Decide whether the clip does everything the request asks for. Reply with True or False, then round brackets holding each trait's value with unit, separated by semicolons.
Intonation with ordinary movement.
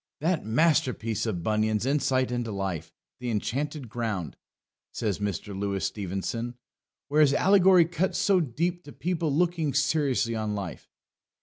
False (6.7 semitones)